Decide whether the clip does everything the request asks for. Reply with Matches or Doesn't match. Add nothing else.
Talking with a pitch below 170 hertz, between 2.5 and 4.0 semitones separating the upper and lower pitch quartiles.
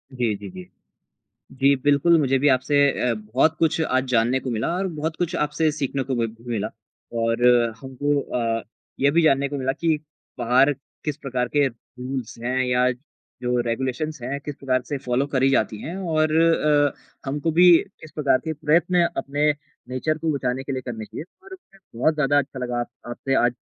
Matches